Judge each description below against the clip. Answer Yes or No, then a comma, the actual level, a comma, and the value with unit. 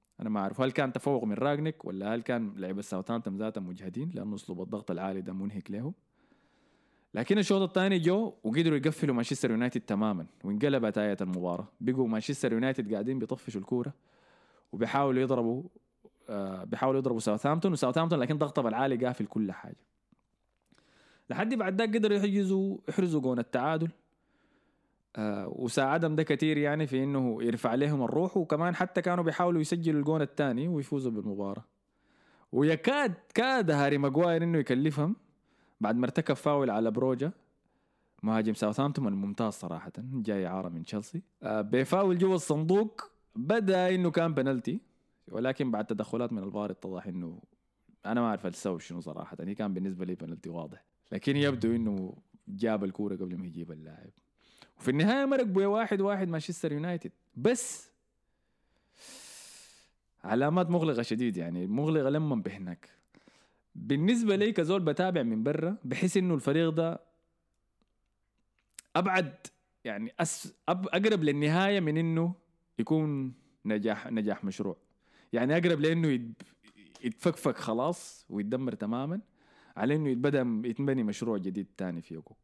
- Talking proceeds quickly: Yes, fast, 140 wpm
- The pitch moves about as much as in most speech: No, wide, 7.7 semitones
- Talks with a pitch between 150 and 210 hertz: No, medium, 140 Hz